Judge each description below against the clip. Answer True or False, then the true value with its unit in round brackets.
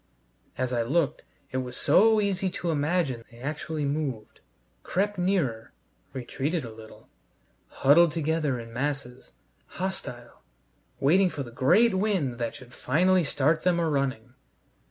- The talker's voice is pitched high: False (145 Hz)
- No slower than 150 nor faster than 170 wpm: False (135 wpm)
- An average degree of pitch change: False (5.9 semitones)